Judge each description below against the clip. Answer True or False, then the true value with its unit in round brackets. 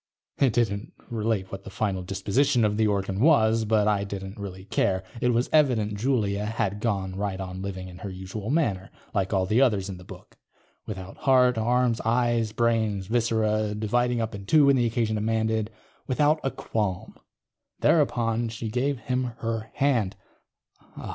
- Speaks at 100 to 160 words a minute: False (175 wpm)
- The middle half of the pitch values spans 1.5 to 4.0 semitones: True (3.3 semitones)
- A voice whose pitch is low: True (110 Hz)